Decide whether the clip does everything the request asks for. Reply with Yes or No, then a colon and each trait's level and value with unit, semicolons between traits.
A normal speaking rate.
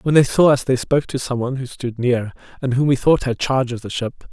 No: fast, 290 wpm